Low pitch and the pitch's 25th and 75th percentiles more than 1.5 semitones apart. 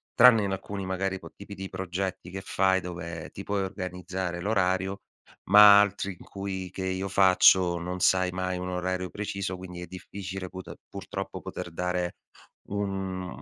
No: very low, 95 Hz; narrow, 1.2 semitones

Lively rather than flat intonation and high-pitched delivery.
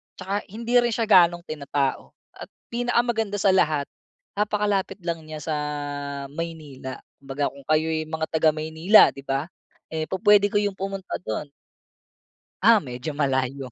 No: wide, 5.8 semitones; medium, 160 Hz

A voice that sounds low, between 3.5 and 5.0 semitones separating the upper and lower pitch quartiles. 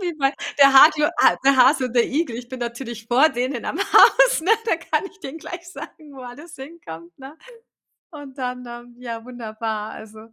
No: very high, 265 Hz; average, 4.3 semitones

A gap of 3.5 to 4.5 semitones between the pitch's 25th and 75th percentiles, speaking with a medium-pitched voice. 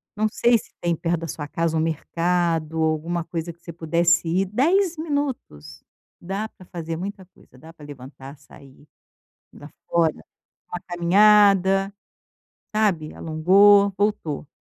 Yes: average, 4.1 semitones; medium, 170 Hz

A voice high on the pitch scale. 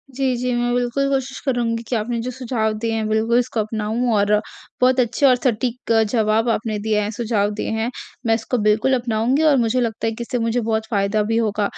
Yes: high, 230 Hz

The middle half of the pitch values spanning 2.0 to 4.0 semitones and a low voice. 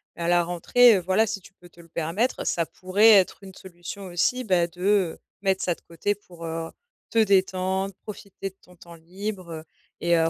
No: average, 2.8 semitones; medium, 185 Hz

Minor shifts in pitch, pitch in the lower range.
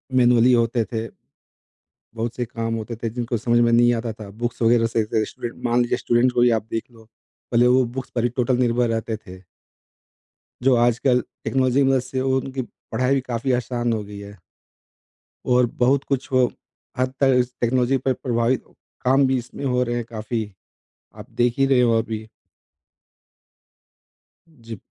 Yes: narrow, 1.9 semitones; low, 120 Hz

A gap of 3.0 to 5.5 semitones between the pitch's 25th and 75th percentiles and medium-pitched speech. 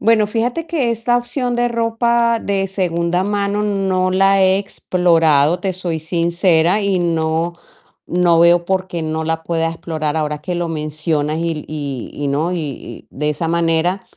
Yes: average, 3.7 semitones; medium, 175 Hz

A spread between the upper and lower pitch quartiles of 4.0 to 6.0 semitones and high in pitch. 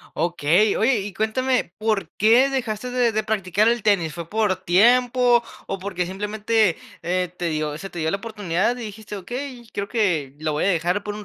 Yes: average, 4.5 semitones; high, 205 Hz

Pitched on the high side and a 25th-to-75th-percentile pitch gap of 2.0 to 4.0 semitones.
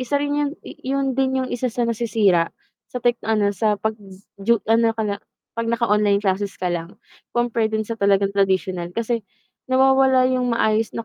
Yes: high, 230 Hz; average, 3.7 semitones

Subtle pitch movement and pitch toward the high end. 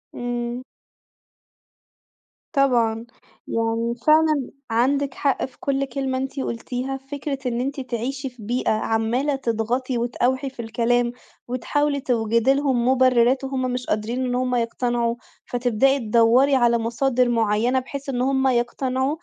Yes: narrow, 2.3 semitones; very high, 250 Hz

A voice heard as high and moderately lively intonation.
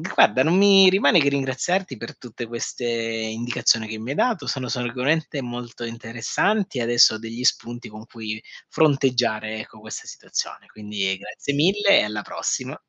No: low, 120 Hz; average, 4.1 semitones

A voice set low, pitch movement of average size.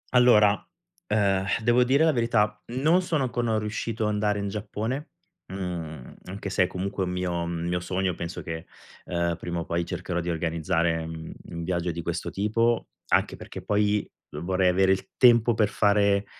Yes: very low, 95 Hz; average, 4.1 semitones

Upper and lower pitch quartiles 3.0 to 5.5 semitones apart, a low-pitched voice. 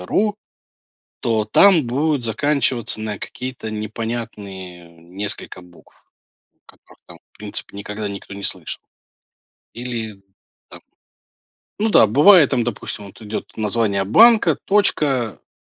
Yes: average, 4.5 semitones; low, 110 Hz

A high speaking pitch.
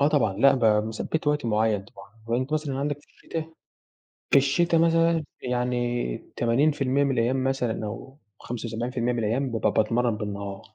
No: low, 125 Hz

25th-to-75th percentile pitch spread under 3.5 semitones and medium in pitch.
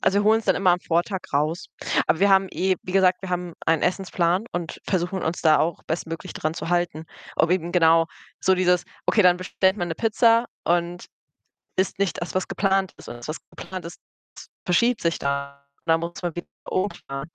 Yes: narrow, 2.5 semitones; medium, 175 Hz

